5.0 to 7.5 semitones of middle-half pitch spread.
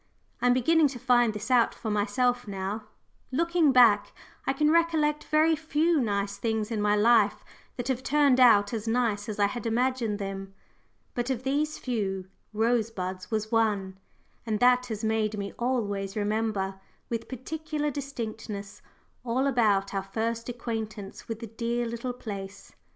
No: average, 3.6 semitones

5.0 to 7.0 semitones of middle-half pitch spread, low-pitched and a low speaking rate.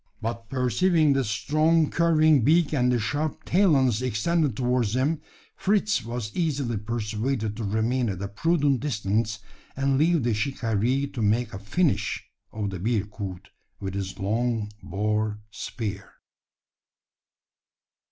Yes: average, 5.3 semitones; low, 120 Hz; slow, 130 wpm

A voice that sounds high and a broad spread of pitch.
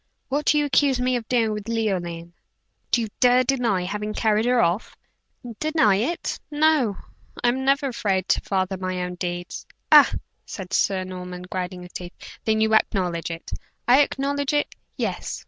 Yes: high, 215 Hz; wide, 5.7 semitones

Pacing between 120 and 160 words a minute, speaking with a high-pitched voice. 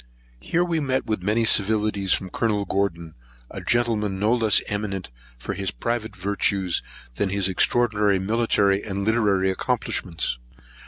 No: average, 140 wpm; low, 100 Hz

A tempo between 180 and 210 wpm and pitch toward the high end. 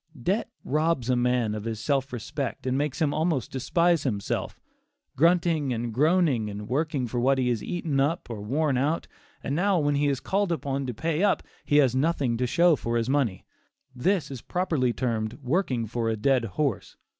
No: average, 190 wpm; low, 135 Hz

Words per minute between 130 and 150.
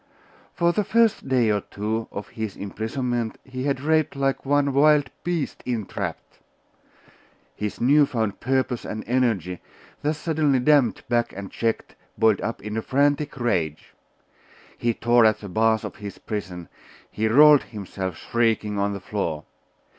Yes: average, 145 wpm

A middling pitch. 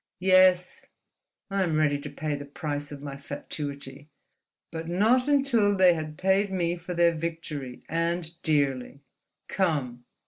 Yes: medium, 165 Hz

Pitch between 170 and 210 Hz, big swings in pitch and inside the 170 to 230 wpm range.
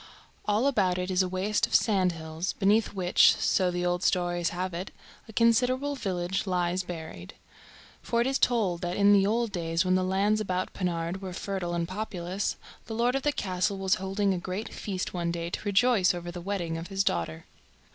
No: medium, 185 Hz; average, 2.8 semitones; average, 195 wpm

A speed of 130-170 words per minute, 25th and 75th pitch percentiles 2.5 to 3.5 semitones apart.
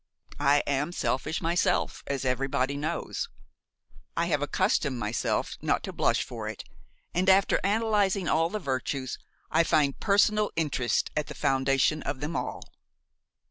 No: average, 140 wpm; average, 5.2 semitones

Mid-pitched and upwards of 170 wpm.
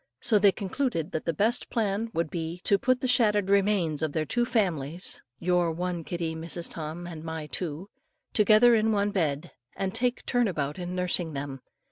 Yes: medium, 180 Hz; average, 185 wpm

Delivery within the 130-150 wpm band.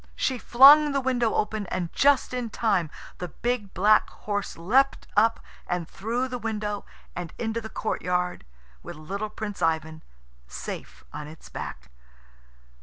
Yes: average, 145 wpm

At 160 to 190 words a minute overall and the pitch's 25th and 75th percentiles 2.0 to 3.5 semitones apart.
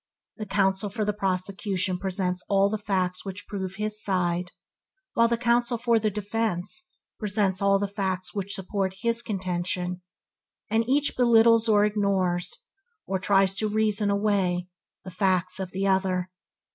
No: average, 145 wpm; narrow, 2.5 semitones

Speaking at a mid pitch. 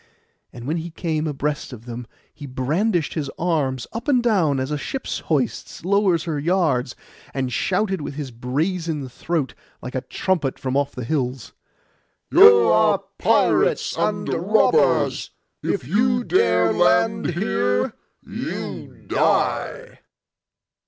Yes: medium, 150 Hz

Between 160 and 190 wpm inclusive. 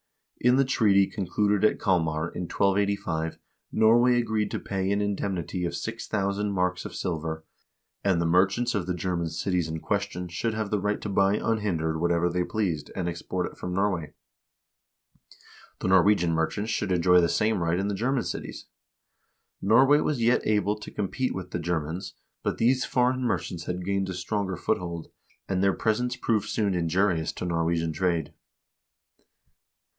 Yes: average, 165 wpm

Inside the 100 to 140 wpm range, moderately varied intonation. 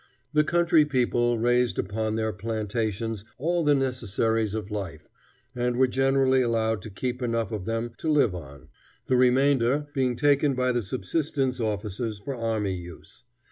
No: average, 155 wpm; average, 3.4 semitones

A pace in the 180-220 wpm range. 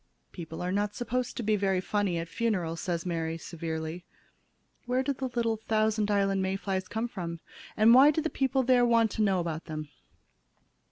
Yes: average, 185 wpm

